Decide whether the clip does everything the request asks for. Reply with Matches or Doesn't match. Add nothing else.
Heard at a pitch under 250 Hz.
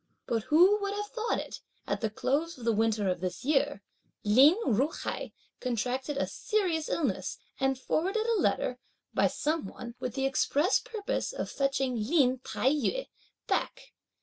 Doesn't match